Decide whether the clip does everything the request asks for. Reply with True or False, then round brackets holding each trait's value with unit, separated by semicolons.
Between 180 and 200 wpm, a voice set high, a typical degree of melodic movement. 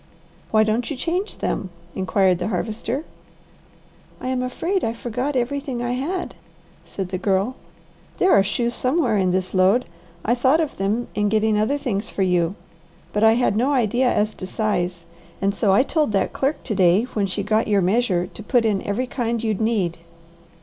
True (185 wpm; 220 Hz; 4.4 semitones)